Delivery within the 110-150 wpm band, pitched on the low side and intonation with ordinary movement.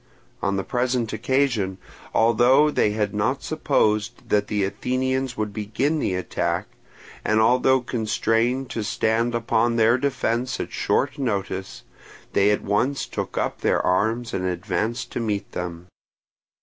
Yes: average, 140 wpm; low, 115 Hz; average, 3.6 semitones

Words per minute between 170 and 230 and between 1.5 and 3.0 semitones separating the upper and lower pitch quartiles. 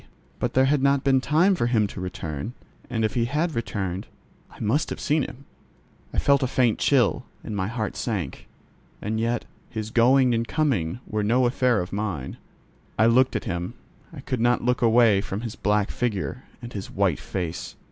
No: average, 190 wpm; average, 4.0 semitones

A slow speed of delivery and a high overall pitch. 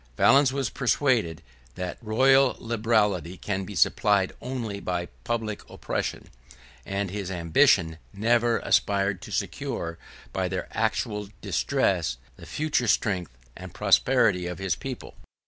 No: slow, 125 wpm; low, 100 Hz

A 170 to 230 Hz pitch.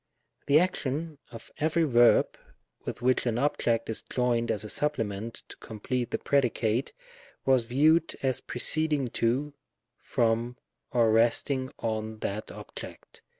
No: low, 125 Hz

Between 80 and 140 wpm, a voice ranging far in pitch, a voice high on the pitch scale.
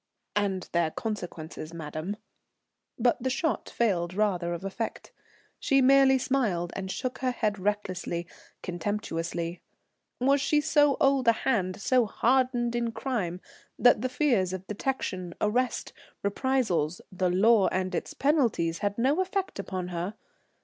Yes: slow, 135 wpm; wide, 6.1 semitones; high, 210 Hz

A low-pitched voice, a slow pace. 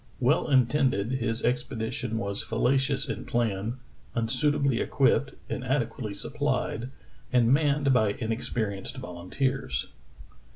Yes: low, 120 Hz; slow, 95 wpm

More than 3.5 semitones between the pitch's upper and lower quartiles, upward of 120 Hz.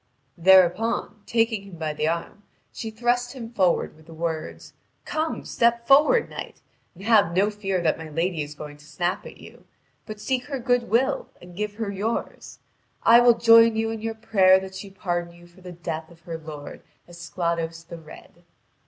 Yes: average, 5.2 semitones; high, 190 Hz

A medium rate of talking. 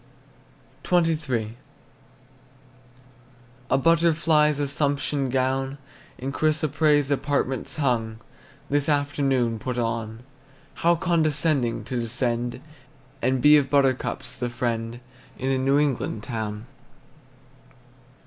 No: slow, 90 wpm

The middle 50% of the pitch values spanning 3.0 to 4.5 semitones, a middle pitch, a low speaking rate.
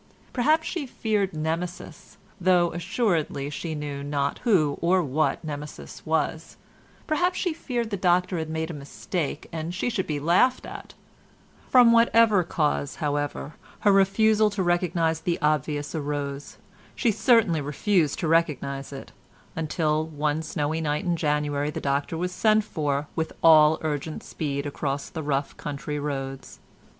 No: average, 4.2 semitones; medium, 160 Hz; average, 145 wpm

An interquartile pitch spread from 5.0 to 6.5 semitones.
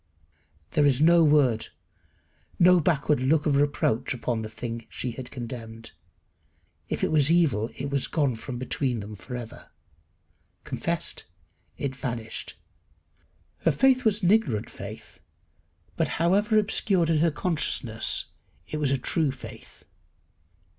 Yes: wide, 5.5 semitones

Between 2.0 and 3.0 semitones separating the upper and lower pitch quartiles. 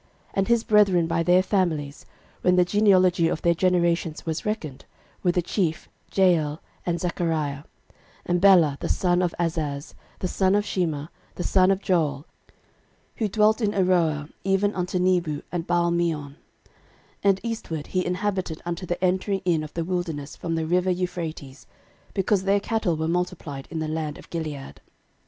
Yes: average, 2.7 semitones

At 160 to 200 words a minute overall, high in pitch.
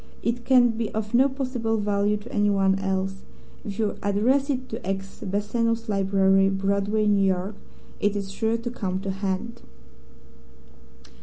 No: average, 150 wpm; high, 205 Hz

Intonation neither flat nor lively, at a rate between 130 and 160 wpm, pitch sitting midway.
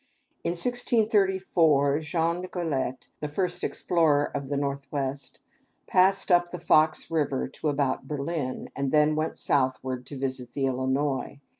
Yes: average, 3.9 semitones; slow, 135 wpm; medium, 150 Hz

